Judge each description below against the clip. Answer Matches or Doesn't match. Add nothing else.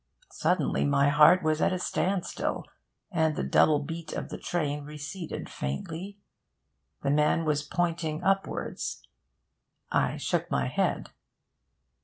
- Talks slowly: Matches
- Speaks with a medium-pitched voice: Matches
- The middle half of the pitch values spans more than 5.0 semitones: Doesn't match